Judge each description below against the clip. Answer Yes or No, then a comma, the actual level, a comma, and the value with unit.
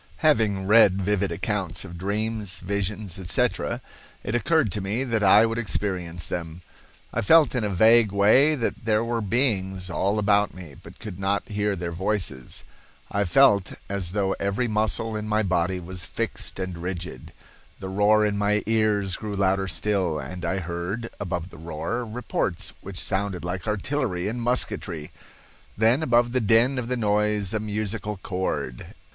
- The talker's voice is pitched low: Yes, low, 100 Hz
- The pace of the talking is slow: No, average, 165 wpm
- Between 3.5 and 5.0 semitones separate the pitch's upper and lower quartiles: No, average, 3.0 semitones